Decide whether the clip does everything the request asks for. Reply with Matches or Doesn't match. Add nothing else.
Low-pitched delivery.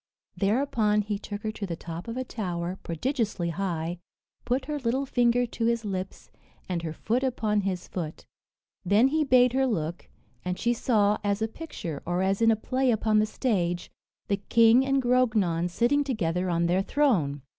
Doesn't match